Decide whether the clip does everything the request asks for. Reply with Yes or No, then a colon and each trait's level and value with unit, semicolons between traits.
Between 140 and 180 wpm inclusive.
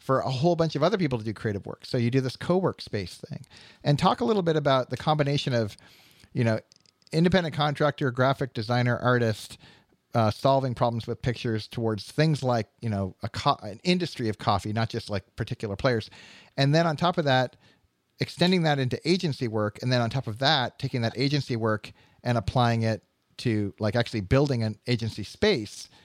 No: average, 200 wpm